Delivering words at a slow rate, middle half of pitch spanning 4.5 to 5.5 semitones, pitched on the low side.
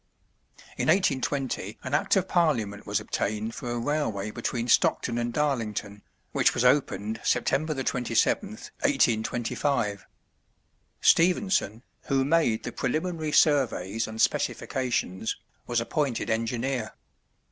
Yes: slow, 110 wpm; average, 5.2 semitones; low, 125 Hz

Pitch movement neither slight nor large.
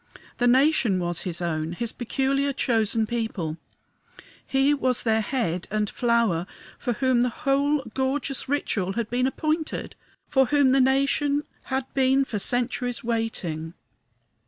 Yes: average, 4.1 semitones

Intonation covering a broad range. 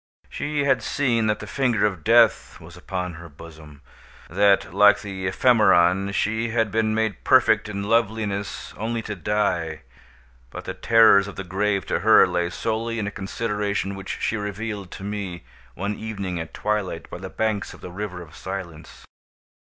No: average, 3.0 semitones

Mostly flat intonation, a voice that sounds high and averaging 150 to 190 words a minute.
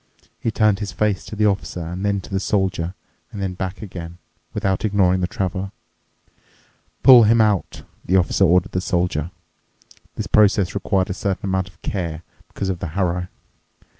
No: narrow, 2.0 semitones; very low, 95 Hz; average, 170 wpm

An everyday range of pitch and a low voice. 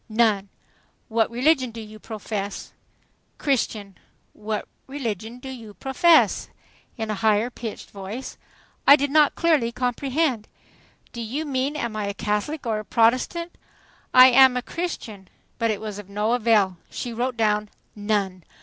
No: average, 3.7 semitones; high, 230 Hz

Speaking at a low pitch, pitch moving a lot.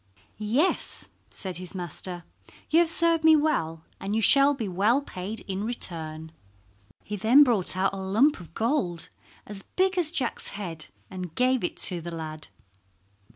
No: high, 200 Hz; wide, 7.6 semitones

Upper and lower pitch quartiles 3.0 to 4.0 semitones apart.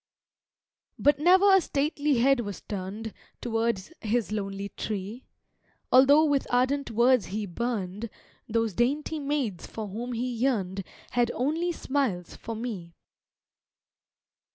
No: average, 5.1 semitones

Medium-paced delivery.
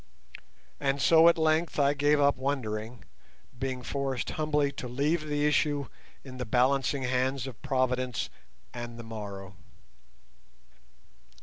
No: slow, 125 wpm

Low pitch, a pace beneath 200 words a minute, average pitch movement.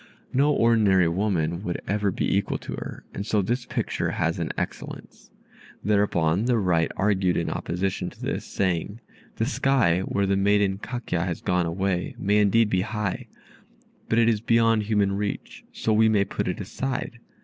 Yes: low, 100 Hz; average, 170 wpm; average, 3.3 semitones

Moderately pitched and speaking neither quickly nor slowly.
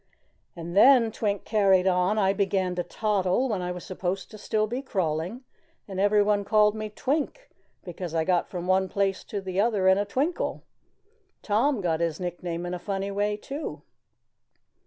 No: high, 195 Hz; average, 170 wpm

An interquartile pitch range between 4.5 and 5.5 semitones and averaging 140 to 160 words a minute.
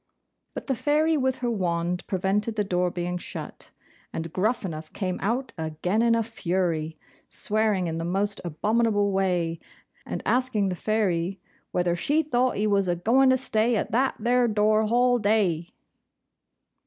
Yes: average, 4.8 semitones; average, 155 wpm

